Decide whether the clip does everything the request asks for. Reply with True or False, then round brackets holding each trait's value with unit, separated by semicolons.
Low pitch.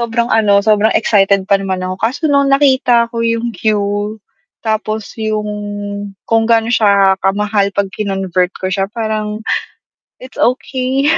False (215 Hz)